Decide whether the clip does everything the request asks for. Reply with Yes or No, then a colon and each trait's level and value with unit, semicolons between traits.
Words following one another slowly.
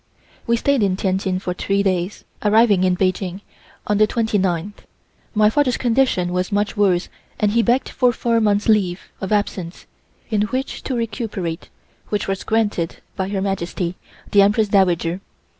No: average, 160 wpm